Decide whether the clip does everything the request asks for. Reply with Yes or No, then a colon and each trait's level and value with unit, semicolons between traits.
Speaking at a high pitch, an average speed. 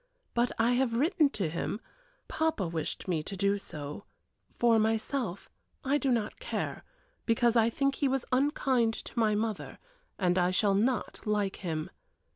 Yes: high, 225 Hz; average, 160 wpm